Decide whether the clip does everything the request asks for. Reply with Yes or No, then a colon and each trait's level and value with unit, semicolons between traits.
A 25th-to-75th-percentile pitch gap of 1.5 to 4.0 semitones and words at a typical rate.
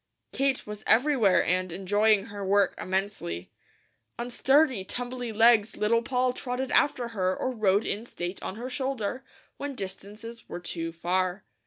No: average, 4.7 semitones; average, 150 wpm